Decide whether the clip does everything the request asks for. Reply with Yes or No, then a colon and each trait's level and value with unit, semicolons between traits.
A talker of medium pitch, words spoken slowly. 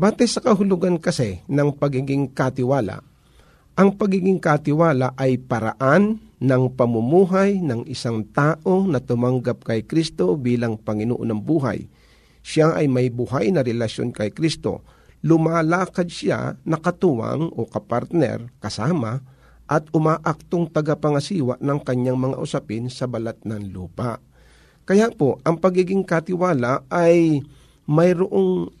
No: medium, 145 Hz; average, 120 wpm